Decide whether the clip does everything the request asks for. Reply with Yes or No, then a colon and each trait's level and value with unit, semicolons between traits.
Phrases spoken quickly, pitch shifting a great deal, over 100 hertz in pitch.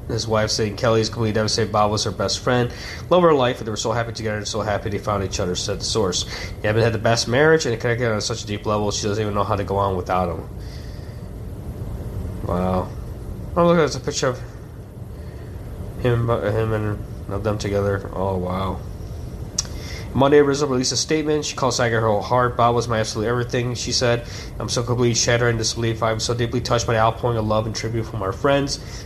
No: fast, 225 wpm; average, 2.9 semitones; low, 110 Hz